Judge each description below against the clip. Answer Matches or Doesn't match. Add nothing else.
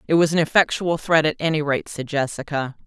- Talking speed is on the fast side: Matches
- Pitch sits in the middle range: Matches